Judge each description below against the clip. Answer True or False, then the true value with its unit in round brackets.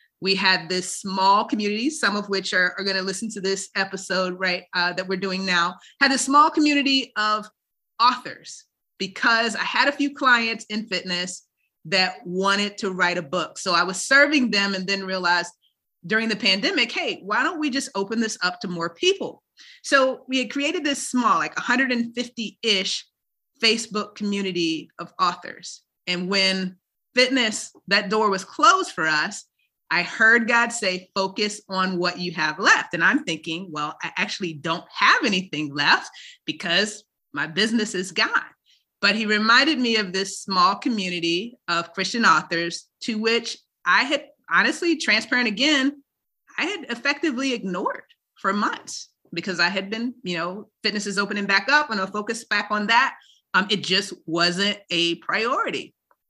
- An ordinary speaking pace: True (165 wpm)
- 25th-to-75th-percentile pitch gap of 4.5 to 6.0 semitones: True (4.9 semitones)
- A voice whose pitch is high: True (205 Hz)